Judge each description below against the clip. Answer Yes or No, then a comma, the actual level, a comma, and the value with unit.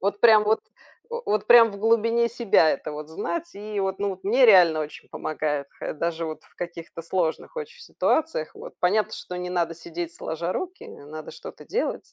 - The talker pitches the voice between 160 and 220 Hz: Yes, high, 190 Hz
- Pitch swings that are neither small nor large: No, wide, 5.7 semitones